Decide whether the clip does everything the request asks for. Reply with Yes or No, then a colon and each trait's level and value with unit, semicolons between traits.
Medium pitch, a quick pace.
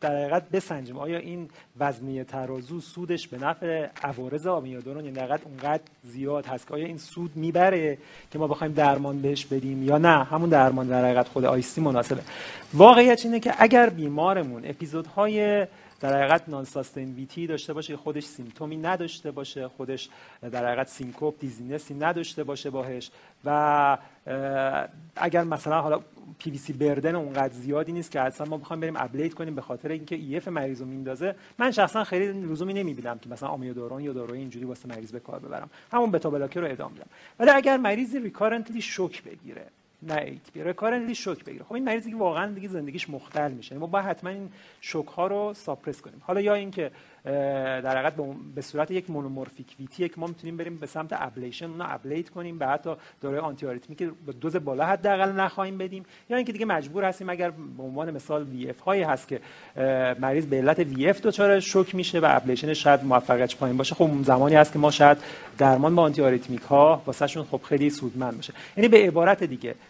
Yes: medium, 150 Hz; fast, 190 wpm